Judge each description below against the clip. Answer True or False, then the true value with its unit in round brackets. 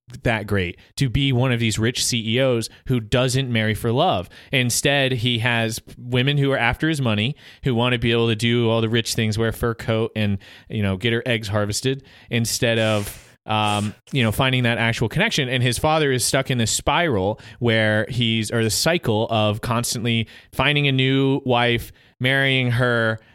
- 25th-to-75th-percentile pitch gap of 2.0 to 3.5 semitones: True (2.8 semitones)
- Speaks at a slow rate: False (195 wpm)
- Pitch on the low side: True (120 Hz)